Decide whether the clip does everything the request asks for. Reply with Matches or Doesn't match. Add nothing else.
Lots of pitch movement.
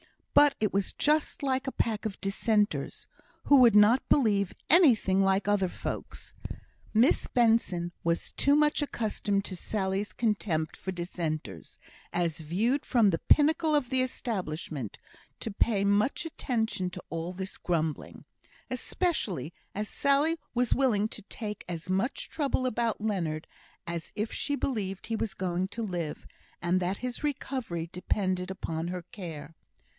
Matches